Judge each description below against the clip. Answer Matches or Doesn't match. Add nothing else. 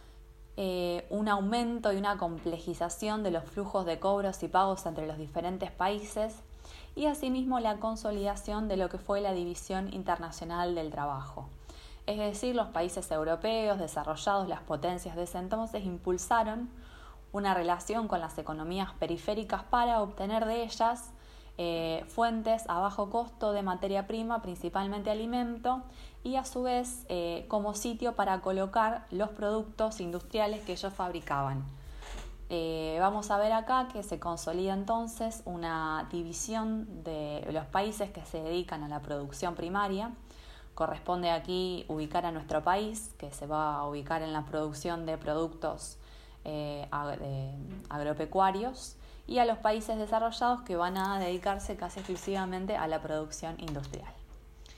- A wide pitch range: Doesn't match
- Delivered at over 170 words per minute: Doesn't match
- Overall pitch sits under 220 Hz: Matches